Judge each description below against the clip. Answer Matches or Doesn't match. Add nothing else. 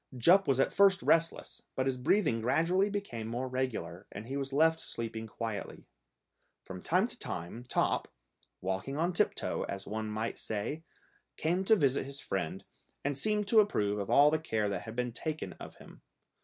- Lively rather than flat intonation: Matches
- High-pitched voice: Doesn't match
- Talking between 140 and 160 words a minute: Doesn't match